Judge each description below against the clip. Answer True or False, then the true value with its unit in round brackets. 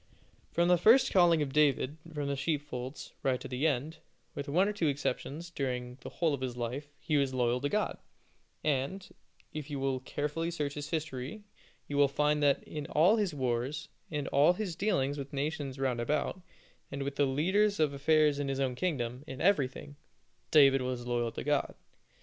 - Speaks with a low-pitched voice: False (145 Hz)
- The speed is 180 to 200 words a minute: True (190 wpm)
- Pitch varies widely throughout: False (3.1 semitones)